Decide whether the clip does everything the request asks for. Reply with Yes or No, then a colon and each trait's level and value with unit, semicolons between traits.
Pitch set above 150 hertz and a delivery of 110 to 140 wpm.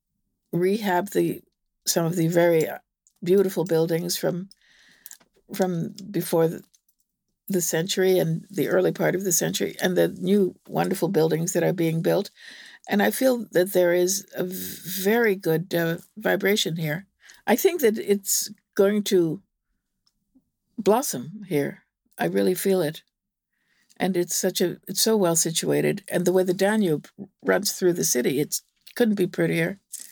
No: medium, 185 Hz; average, 150 wpm